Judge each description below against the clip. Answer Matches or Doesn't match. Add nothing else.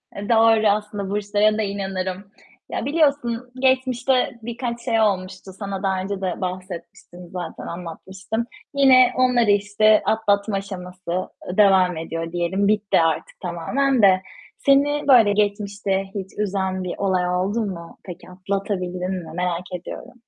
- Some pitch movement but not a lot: Matches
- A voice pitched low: Doesn't match